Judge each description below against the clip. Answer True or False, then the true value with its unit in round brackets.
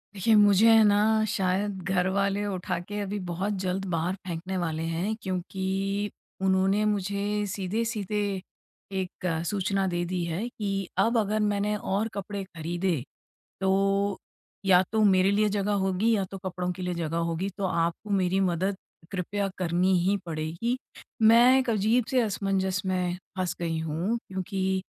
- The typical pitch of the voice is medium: False (195 Hz)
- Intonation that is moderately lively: False (2.1 semitones)